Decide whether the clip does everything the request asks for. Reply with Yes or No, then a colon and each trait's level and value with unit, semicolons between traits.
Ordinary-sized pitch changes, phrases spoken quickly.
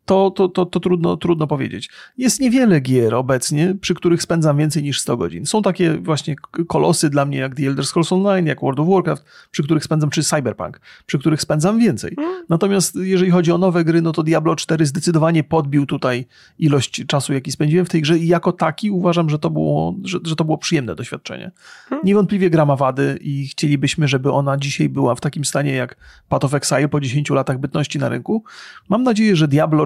Yes: average, 4.0 semitones; fast, 205 wpm